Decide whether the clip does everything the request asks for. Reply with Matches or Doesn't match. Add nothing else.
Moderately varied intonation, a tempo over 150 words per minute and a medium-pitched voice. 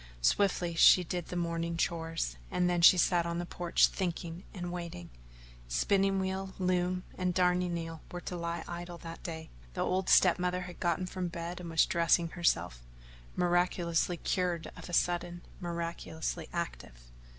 Doesn't match